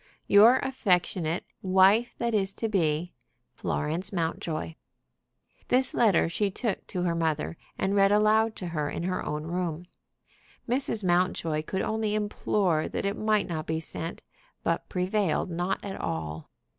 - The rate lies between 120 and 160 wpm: Yes, average, 145 wpm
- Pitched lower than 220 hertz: Yes, medium, 185 Hz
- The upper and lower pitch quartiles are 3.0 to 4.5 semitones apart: Yes, average, 4.2 semitones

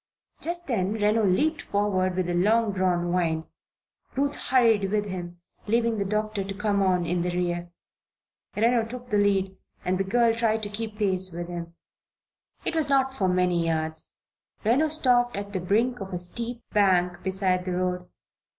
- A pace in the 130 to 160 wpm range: No, average, 175 wpm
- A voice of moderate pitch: No, high, 200 Hz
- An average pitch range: Yes, average, 4.0 semitones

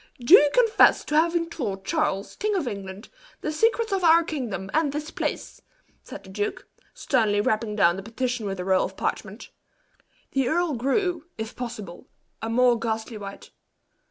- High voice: Yes, high, 245 Hz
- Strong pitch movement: Yes, wide, 7.7 semitones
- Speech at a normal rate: Yes, average, 170 wpm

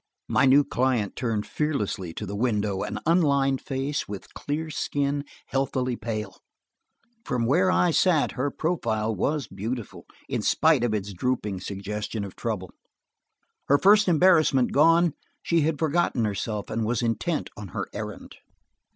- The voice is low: Yes, low, 130 Hz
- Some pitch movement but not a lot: No, wide, 6.1 semitones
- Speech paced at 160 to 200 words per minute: No, average, 150 wpm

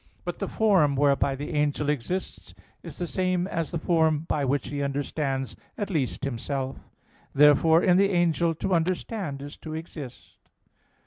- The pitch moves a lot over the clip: No, average, 3.8 semitones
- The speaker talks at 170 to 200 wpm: No, average, 155 wpm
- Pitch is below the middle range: No, medium, 155 Hz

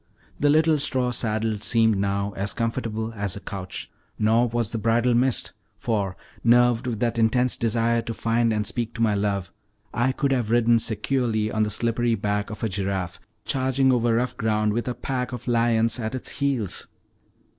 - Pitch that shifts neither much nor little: No, narrow, 2.3 semitones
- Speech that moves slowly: No, average, 180 wpm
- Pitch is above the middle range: No, low, 115 Hz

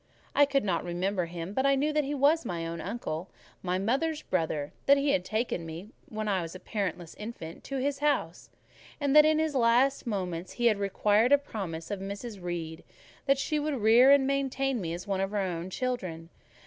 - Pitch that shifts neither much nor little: No, wide, 7.5 semitones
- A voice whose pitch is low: No, high, 215 Hz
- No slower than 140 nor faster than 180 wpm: No, average, 195 wpm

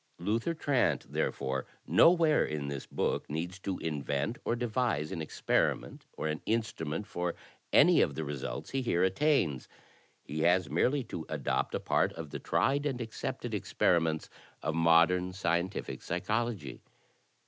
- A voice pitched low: Yes, very low, 90 Hz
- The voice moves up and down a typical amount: No, wide, 7.1 semitones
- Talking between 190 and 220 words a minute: No, average, 145 wpm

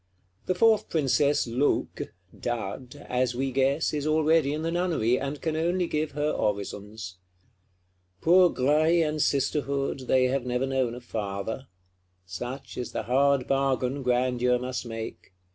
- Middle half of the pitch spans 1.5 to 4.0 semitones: Yes, average, 3.6 semitones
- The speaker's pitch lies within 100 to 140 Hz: Yes, low, 135 Hz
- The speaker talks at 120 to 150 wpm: Yes, average, 145 wpm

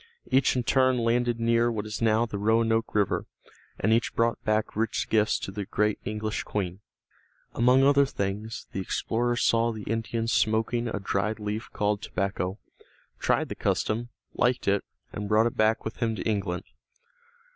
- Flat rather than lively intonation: Yes, narrow, 2.0 semitones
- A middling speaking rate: Yes, average, 165 wpm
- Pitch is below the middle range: Yes, low, 110 Hz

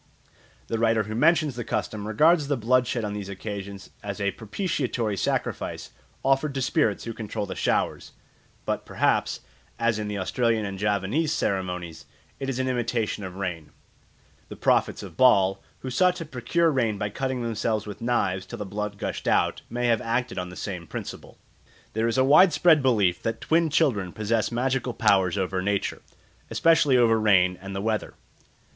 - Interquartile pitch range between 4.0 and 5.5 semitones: Yes, average, 4.3 semitones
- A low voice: Yes, low, 110 Hz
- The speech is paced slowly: No, average, 175 wpm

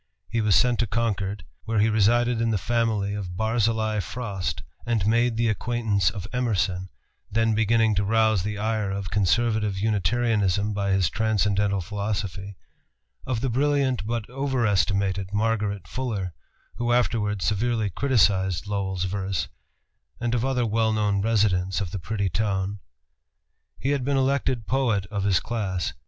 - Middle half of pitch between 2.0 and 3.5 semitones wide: Yes, average, 2.8 semitones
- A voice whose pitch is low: Yes, low, 105 Hz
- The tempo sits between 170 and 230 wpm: No, average, 145 wpm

